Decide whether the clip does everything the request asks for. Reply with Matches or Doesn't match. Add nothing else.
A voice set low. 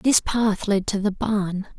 Doesn't match